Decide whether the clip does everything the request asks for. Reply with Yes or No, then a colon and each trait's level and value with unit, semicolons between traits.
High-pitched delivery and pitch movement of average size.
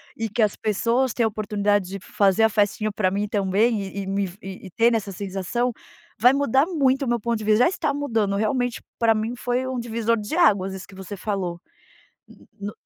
Yes: high, 215 Hz; average, 3.2 semitones